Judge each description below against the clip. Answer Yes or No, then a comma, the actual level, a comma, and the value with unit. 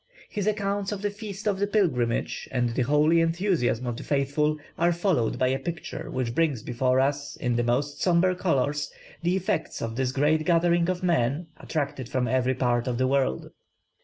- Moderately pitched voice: Yes, medium, 145 Hz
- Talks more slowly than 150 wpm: No, average, 190 wpm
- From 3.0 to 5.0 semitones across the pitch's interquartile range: No, wide, 5.6 semitones